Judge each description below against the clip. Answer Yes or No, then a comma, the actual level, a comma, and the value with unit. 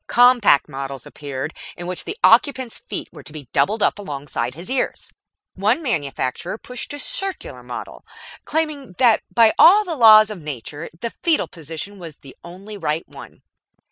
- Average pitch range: No, wide, 8.9 semitones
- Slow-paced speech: No, average, 165 wpm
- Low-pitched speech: No, high, 200 Hz